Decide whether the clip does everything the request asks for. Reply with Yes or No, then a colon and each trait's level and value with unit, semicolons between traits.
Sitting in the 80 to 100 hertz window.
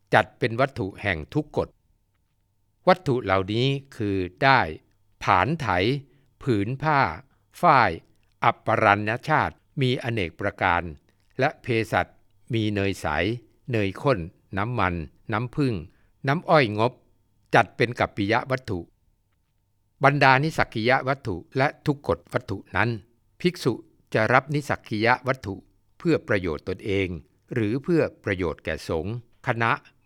No: low, 110 Hz